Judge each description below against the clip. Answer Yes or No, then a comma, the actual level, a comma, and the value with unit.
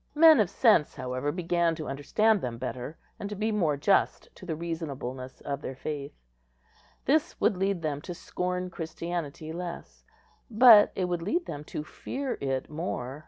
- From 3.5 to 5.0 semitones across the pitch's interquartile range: No, wide, 5.6 semitones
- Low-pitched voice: No, medium, 170 Hz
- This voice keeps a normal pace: Yes, average, 165 wpm